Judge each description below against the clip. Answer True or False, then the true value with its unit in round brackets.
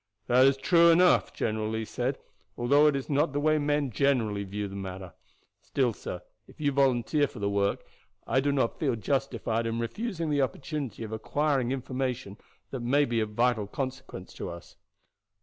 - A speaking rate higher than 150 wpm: True (180 wpm)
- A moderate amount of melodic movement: True (4.4 semitones)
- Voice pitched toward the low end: True (130 Hz)